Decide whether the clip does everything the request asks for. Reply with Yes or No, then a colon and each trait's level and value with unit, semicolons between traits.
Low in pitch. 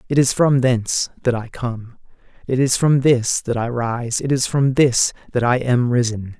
Yes: low, 125 Hz